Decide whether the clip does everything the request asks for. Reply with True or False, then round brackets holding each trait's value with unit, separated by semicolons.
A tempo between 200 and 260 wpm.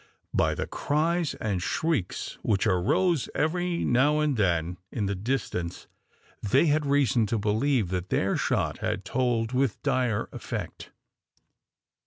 False (135 wpm)